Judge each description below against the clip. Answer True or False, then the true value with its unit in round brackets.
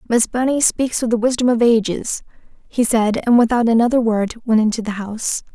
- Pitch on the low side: False (230 Hz)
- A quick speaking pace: False (195 wpm)